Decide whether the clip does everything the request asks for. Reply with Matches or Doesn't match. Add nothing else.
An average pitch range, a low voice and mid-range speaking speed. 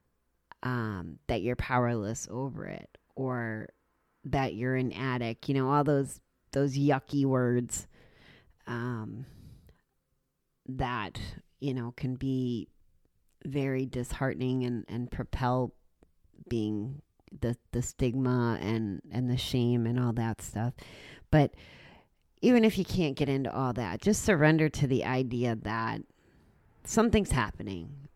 Doesn't match